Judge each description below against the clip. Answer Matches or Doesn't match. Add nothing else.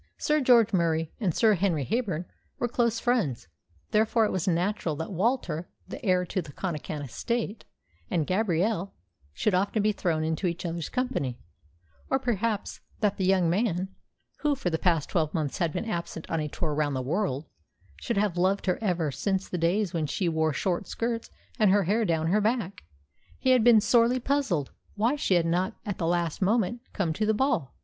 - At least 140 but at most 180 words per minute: Doesn't match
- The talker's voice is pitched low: Doesn't match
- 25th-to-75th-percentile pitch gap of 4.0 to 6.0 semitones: Matches